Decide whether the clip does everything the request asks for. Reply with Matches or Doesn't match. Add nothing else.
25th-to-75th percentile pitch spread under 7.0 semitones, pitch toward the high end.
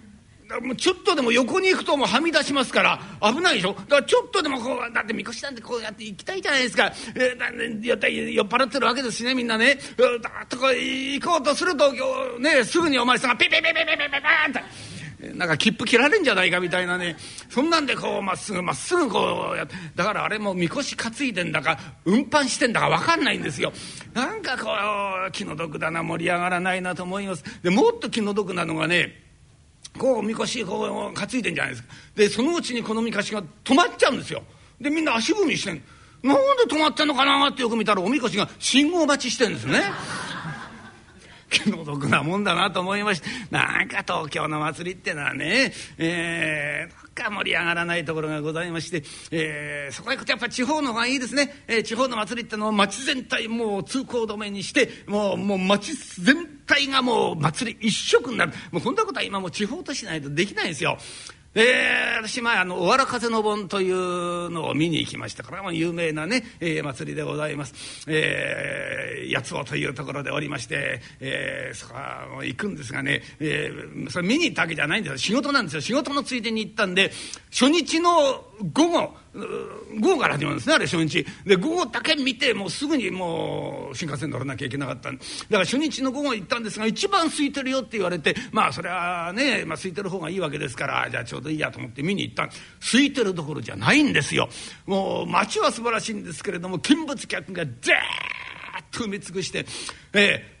Doesn't match